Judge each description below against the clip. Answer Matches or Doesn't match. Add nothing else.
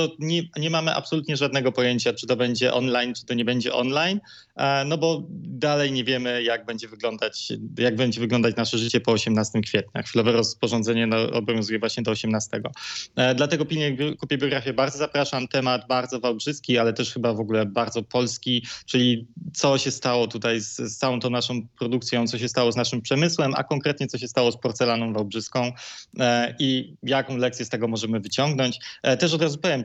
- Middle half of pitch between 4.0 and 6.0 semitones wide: Doesn't match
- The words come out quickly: Matches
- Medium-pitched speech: Doesn't match